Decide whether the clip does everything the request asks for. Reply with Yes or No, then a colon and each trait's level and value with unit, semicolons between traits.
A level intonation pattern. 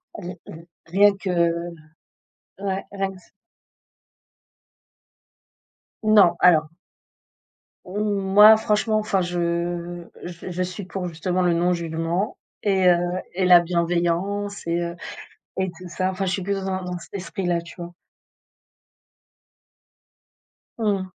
Yes: narrow, 2.3 semitones